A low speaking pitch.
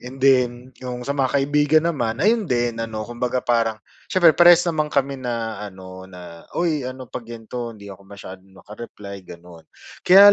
Yes: low, 120 Hz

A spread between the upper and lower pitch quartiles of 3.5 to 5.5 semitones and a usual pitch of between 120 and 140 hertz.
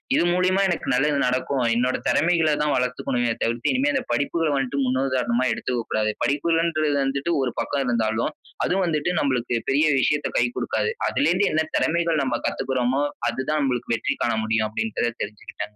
Yes: average, 4.5 semitones; low, 135 Hz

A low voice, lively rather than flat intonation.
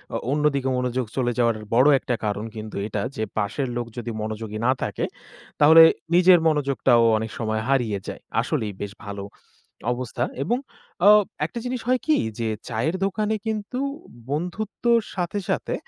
Yes: low, 130 Hz; wide, 8.3 semitones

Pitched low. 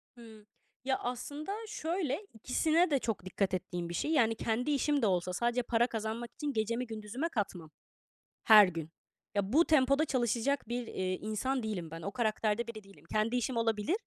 No: high, 230 Hz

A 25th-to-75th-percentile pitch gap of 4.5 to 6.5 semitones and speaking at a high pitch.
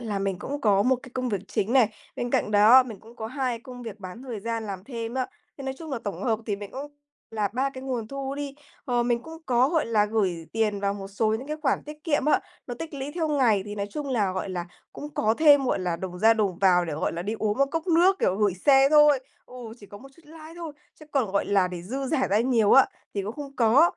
Yes: average, 5.1 semitones; high, 235 Hz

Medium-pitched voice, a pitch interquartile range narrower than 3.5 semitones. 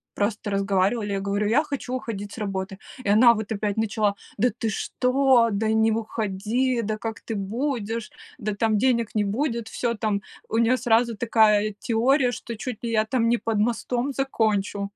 No: high, 225 Hz; narrow, 2.5 semitones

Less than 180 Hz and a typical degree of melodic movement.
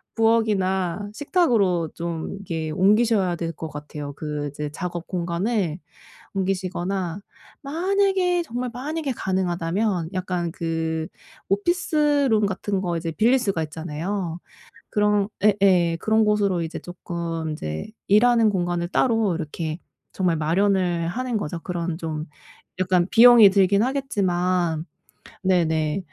No: medium, 185 Hz; average, 4.2 semitones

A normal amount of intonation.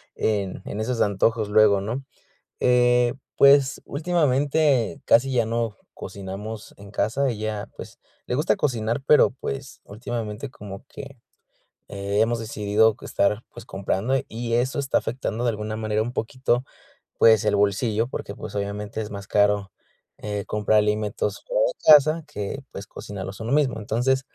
Yes: average, 3.7 semitones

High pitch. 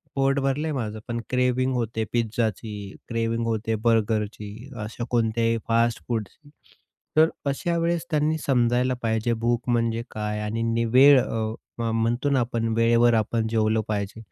No: low, 115 Hz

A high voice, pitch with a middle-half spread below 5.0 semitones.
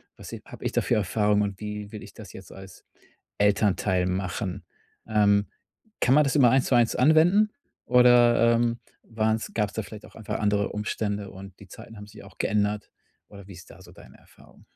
No: low, 105 Hz; narrow, 2.6 semitones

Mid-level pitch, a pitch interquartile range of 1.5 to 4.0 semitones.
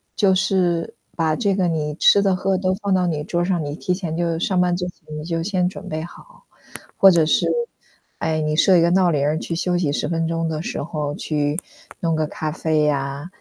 Yes: medium, 170 Hz; average, 2.8 semitones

